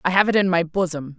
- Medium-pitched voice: Yes, medium, 180 Hz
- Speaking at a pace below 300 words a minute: No, fast, 305 wpm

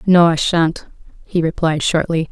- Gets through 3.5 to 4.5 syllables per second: Yes, 4.4 syllables/s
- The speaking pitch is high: No, medium, 165 Hz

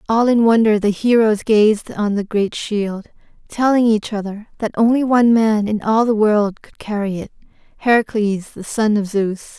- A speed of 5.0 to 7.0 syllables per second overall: No, 4.6 syllables/s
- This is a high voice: Yes, high, 215 Hz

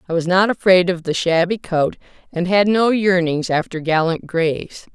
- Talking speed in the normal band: Yes, average, 180 wpm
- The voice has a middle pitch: Yes, medium, 180 Hz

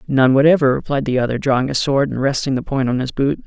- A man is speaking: Yes, male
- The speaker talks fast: Yes, fast, 260 wpm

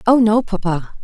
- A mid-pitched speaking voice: No, high, 210 Hz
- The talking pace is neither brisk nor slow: Yes, average, 175 wpm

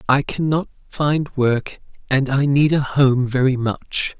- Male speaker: Yes, male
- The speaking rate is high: No, average, 155 wpm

